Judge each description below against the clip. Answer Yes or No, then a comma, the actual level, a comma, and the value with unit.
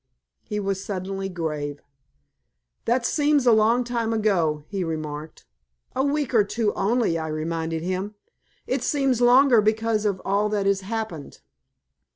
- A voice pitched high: Yes, high, 205 Hz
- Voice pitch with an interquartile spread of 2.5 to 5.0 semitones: No, wide, 5.5 semitones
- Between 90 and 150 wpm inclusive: Yes, average, 145 wpm